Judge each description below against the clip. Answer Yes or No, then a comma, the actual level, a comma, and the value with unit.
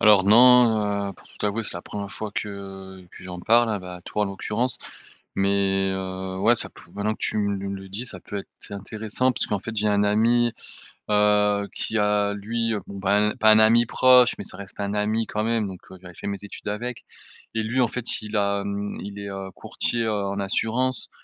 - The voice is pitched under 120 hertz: Yes, low, 105 Hz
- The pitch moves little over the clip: Yes, narrow, 2.1 semitones